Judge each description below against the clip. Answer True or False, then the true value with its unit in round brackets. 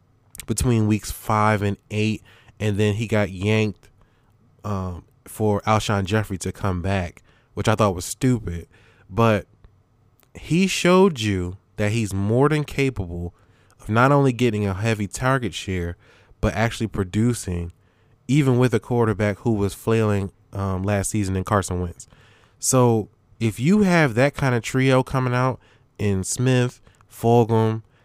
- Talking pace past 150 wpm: False (145 wpm)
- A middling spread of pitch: True (3.2 semitones)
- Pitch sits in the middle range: False (110 Hz)